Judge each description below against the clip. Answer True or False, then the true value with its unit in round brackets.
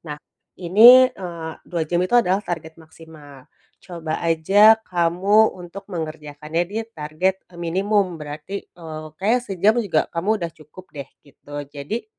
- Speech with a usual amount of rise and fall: True (4.0 semitones)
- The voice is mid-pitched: True (175 Hz)